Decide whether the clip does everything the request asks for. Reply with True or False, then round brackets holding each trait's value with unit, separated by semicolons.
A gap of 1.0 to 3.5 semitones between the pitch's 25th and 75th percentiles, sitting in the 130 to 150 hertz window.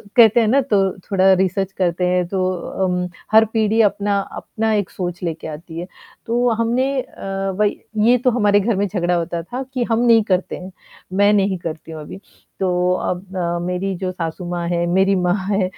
False (2.9 semitones; 190 Hz)